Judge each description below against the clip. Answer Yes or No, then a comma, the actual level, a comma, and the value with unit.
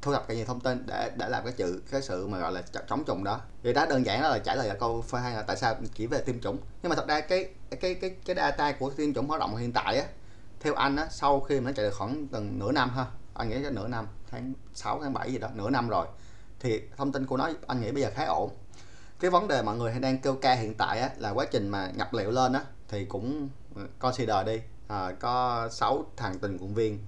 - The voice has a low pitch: Yes, low, 120 Hz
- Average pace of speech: No, fast, 275 wpm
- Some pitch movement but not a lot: Yes, average, 4.2 semitones